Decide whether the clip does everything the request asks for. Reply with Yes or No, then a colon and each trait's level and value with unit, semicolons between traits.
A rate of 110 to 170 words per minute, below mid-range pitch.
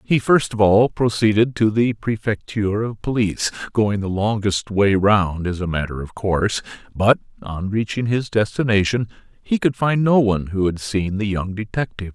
No: average, 180 wpm; low, 105 Hz